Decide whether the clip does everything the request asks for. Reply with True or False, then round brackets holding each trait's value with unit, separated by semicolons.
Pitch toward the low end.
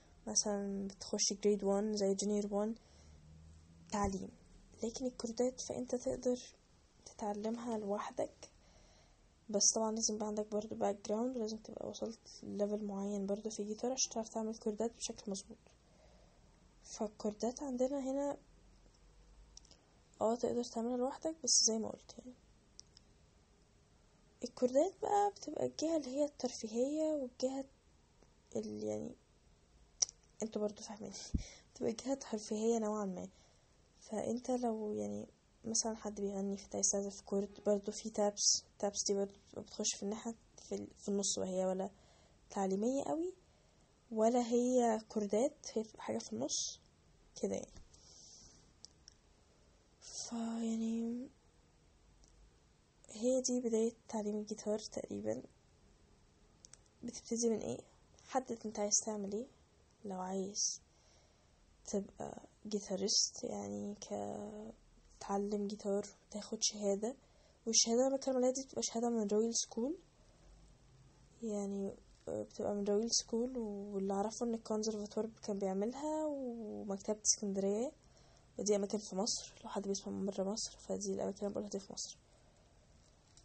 False (215 Hz)